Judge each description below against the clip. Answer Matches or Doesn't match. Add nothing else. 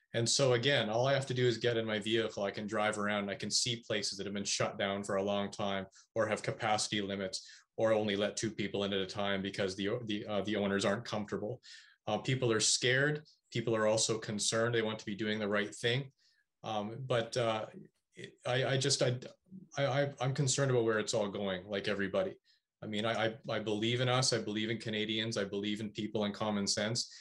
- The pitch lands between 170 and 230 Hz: Doesn't match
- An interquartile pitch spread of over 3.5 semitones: Doesn't match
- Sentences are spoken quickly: Matches